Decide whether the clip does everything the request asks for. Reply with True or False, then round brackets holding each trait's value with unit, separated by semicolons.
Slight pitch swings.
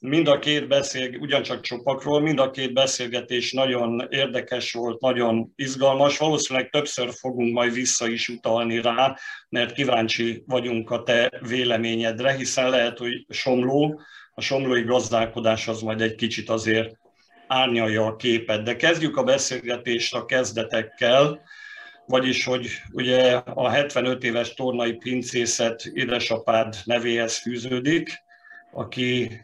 True (2.3 semitones)